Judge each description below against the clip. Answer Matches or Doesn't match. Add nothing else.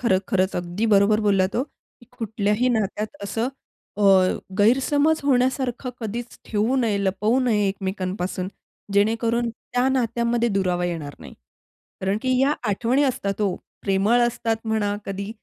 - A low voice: Doesn't match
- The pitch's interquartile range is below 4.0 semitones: Matches